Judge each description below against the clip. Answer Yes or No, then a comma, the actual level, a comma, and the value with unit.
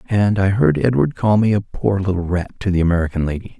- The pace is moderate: No, fast, 235 wpm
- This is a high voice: No, low, 100 Hz